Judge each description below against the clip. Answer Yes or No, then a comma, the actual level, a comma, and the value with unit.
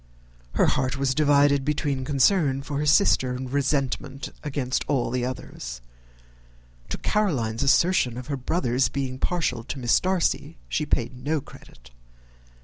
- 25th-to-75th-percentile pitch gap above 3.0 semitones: No, average, 2.7 semitones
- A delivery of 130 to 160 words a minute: Yes, average, 140 wpm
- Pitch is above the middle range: No, medium, 140 Hz